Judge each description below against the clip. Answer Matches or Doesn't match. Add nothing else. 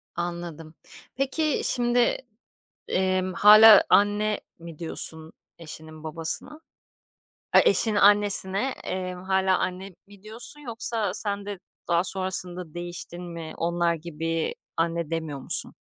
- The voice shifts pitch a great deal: Doesn't match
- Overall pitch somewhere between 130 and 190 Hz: Matches